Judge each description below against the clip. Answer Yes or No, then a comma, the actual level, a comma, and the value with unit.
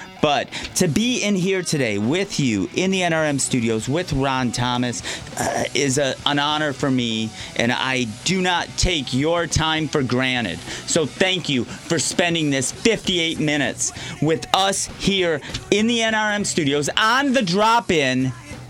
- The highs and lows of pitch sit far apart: Yes, wide, 6.3 semitones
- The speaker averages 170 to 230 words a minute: No, average, 160 wpm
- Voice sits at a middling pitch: Yes, medium, 150 Hz